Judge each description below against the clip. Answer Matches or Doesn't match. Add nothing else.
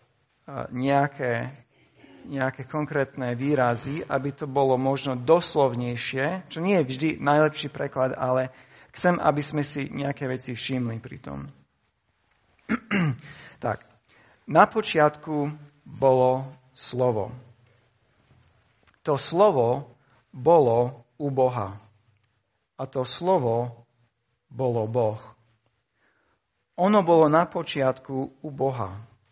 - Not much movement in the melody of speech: Doesn't match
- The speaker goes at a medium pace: Doesn't match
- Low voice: Matches